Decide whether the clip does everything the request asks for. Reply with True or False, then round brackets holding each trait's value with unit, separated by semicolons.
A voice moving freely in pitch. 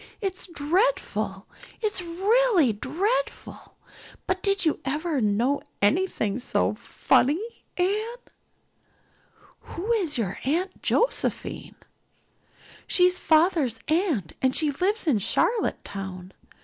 True (7.3 semitones)